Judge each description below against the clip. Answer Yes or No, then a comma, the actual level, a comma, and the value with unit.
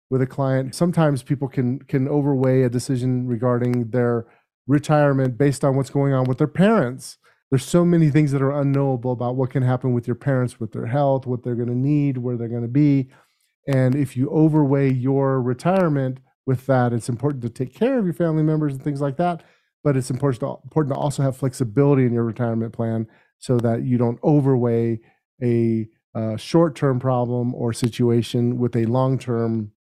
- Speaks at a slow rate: No, average, 190 wpm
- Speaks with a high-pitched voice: No, low, 130 Hz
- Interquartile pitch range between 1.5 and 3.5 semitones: Yes, average, 2.7 semitones